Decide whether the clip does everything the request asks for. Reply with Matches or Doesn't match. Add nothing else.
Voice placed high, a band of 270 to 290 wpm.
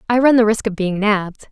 Matches